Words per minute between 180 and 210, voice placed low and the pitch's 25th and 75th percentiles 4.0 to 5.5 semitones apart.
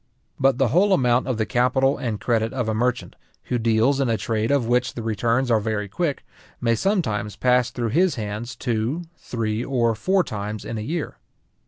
No: average, 195 wpm; low, 120 Hz; average, 3.3 semitones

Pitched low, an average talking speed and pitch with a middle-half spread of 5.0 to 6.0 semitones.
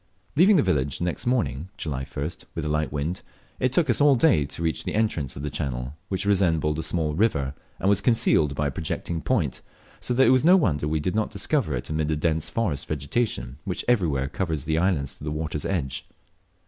No: very low, 80 Hz; fast, 220 wpm; wide, 5.4 semitones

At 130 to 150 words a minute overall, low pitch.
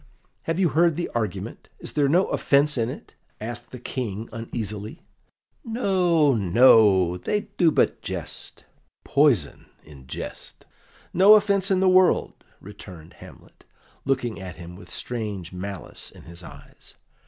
Yes: average, 140 wpm; low, 120 Hz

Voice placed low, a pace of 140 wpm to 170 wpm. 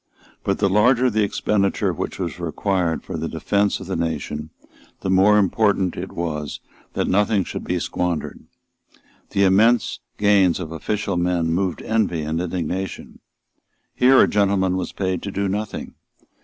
Yes: very low, 95 Hz; average, 155 wpm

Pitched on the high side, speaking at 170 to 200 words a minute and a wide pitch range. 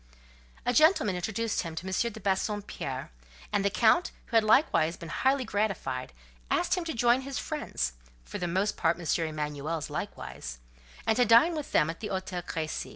Yes: high, 195 Hz; average, 180 wpm; wide, 6.3 semitones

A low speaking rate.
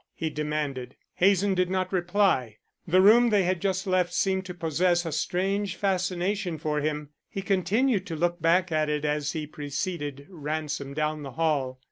No: average, 170 wpm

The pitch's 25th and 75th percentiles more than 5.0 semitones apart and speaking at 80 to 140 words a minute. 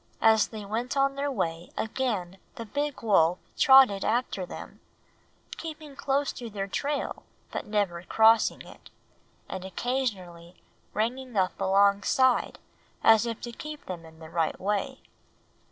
Yes: wide, 5.6 semitones; slow, 135 wpm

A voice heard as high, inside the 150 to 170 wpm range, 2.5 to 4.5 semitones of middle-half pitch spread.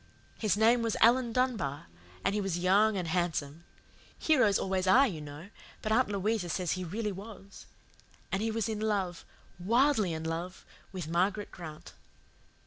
Yes: high, 195 Hz; average, 160 wpm; average, 4.0 semitones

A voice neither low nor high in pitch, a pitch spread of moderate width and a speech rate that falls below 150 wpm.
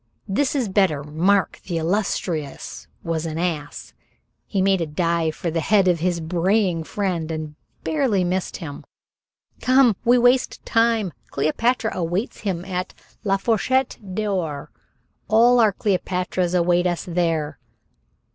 Yes: medium, 180 Hz; average, 4.3 semitones; slow, 135 wpm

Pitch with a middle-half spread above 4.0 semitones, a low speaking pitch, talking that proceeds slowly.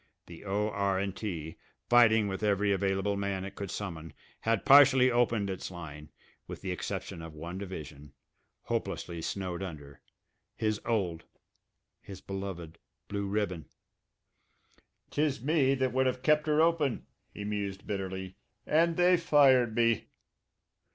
Yes: average, 4.7 semitones; low, 100 Hz; slow, 130 wpm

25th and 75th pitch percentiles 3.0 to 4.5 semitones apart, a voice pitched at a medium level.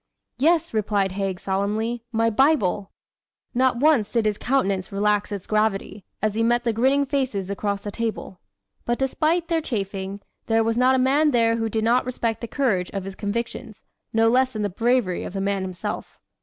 No: average, 4.1 semitones; high, 225 Hz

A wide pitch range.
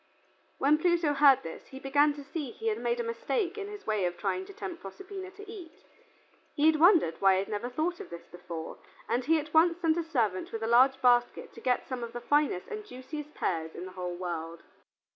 Yes: wide, 8.2 semitones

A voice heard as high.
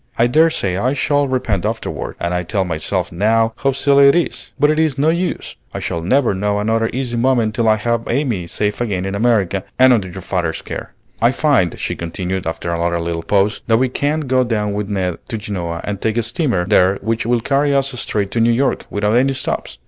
No: low, 110 Hz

